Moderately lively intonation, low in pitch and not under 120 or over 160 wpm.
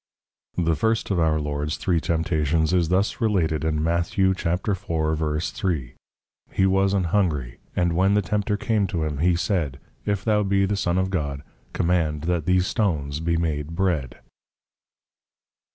Yes: average, 3.6 semitones; very low, 85 Hz; average, 155 wpm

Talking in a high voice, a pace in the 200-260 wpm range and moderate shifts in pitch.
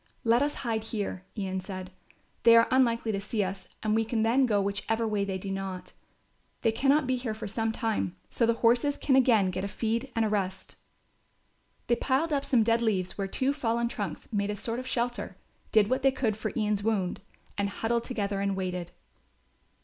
Yes: high, 220 Hz; fast, 205 wpm; average, 3.1 semitones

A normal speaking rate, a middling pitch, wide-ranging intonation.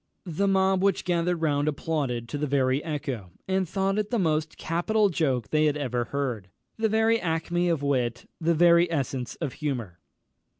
No: average, 180 wpm; medium, 160 Hz; average, 4.6 semitones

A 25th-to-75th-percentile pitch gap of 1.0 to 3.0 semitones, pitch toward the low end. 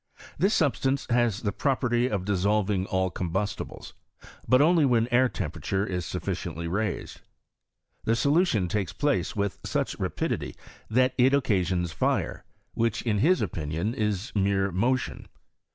No: average, 5.1 semitones; low, 105 Hz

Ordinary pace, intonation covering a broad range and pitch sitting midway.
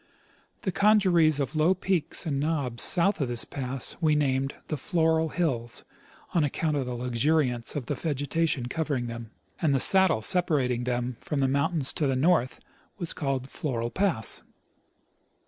No: average, 160 wpm; average, 4.4 semitones; medium, 145 Hz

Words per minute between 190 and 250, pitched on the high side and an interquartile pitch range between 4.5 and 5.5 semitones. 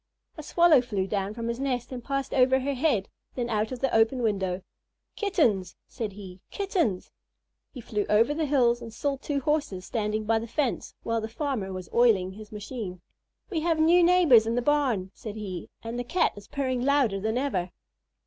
Yes: average, 195 wpm; high, 235 Hz; average, 5.0 semitones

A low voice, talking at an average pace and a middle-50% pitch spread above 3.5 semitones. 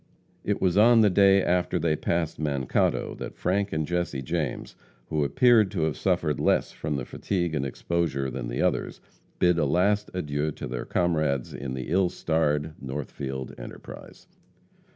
Yes: very low, 80 Hz; average, 165 wpm; average, 4.5 semitones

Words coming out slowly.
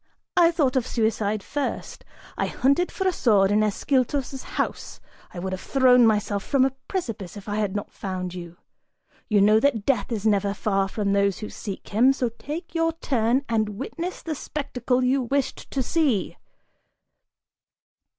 No: average, 170 wpm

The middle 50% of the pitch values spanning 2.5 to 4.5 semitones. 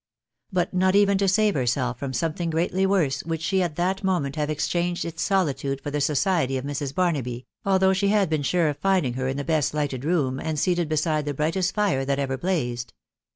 No: average, 5.0 semitones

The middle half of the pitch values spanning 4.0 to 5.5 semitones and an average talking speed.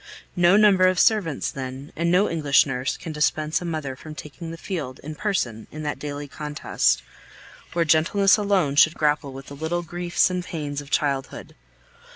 No: average, 3.6 semitones; average, 180 wpm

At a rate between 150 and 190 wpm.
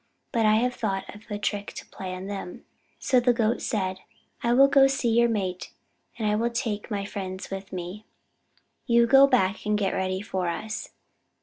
No: average, 200 wpm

